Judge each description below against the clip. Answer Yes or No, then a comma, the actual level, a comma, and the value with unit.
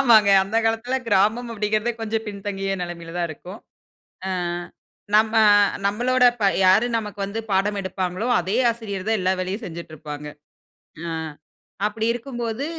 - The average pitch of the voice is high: Yes, high, 210 Hz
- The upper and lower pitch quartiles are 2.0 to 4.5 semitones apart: Yes, average, 3.1 semitones